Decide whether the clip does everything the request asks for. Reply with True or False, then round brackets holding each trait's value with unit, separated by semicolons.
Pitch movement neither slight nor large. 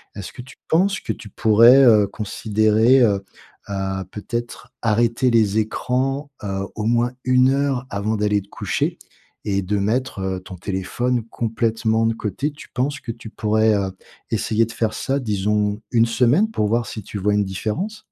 True (3.2 semitones)